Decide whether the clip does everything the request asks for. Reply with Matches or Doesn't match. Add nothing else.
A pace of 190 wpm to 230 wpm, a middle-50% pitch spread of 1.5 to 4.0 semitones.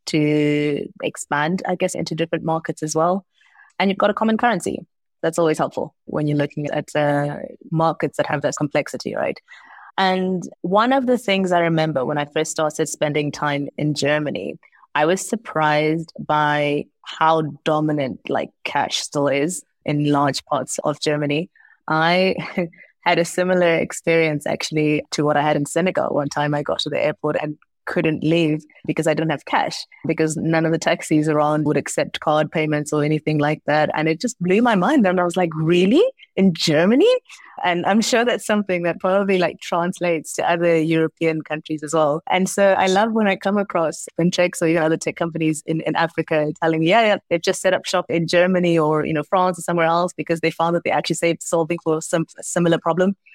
Matches